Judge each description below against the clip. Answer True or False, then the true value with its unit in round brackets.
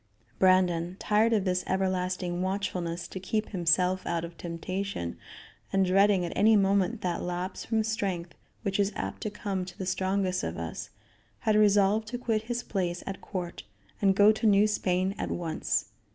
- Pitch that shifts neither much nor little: False (2.3 semitones)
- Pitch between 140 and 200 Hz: True (190 Hz)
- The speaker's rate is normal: True (170 wpm)